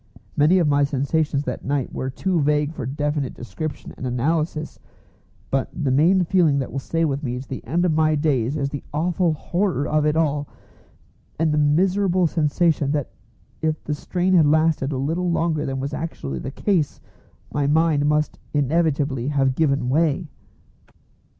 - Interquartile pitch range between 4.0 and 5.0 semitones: No, average, 2.7 semitones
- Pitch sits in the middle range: Yes, medium, 150 Hz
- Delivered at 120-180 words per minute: Yes, average, 170 wpm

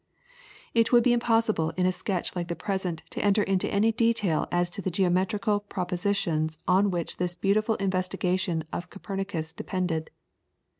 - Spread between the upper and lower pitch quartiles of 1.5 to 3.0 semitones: Yes, average, 2.7 semitones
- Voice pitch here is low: No, medium, 185 Hz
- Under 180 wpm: Yes, average, 160 wpm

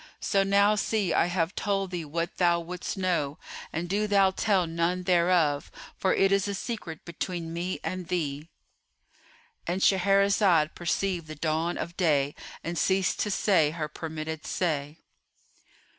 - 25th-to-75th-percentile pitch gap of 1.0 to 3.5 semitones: Yes, average, 3.0 semitones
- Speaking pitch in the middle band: Yes, medium, 175 Hz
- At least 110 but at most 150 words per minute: Yes, average, 145 wpm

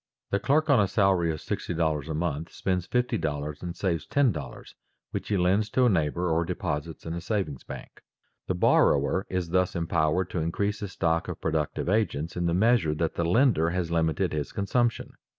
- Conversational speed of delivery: Yes, average, 185 wpm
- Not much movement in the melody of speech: No, average, 3.7 semitones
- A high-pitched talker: No, very low, 85 Hz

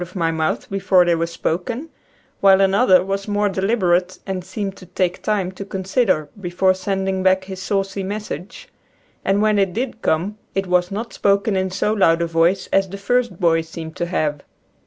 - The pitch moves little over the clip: Yes, narrow, 2.0 semitones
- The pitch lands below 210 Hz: Yes, high, 190 Hz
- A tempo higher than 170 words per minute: Yes, average, 185 wpm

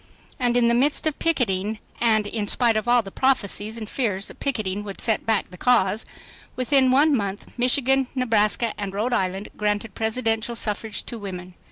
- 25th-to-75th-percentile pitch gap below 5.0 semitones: Yes, average, 3.3 semitones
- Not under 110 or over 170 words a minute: No, average, 180 wpm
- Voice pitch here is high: Yes, high, 225 Hz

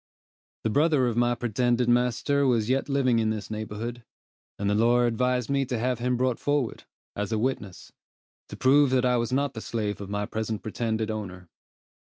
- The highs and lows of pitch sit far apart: No, average, 2.7 semitones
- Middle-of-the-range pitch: No, low, 120 Hz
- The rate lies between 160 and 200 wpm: Yes, average, 190 wpm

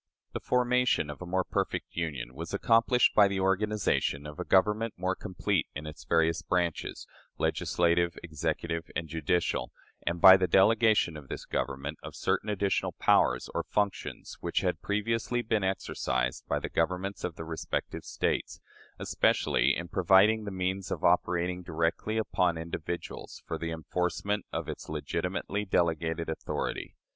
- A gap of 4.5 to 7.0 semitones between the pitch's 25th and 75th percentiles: No, average, 3.7 semitones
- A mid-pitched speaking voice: No, very low, 90 Hz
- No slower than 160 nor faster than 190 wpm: No, average, 150 wpm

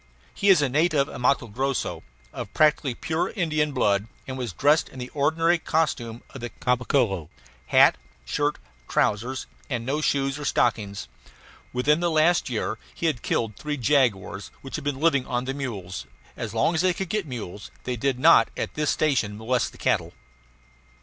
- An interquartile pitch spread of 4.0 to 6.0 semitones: Yes, average, 4.4 semitones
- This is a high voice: No, low, 135 Hz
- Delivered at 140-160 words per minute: No, average, 175 wpm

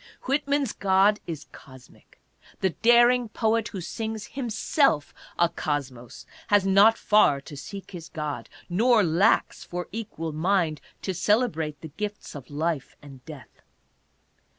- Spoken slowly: Yes, slow, 130 wpm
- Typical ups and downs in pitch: No, wide, 6.2 semitones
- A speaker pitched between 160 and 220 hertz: Yes, high, 190 Hz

